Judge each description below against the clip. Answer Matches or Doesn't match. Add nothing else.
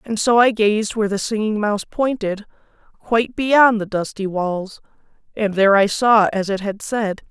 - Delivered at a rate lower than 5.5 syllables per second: Matches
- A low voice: Doesn't match